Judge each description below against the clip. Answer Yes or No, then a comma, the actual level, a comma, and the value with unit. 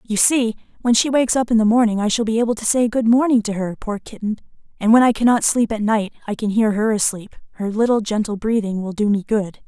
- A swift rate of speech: Yes, fast, 255 wpm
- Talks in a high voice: Yes, high, 220 Hz